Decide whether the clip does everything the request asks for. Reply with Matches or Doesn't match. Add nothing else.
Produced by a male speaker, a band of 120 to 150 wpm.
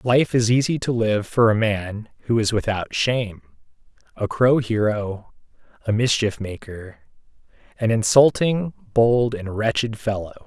Matches